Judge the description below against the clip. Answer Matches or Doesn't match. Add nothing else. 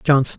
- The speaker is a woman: Doesn't match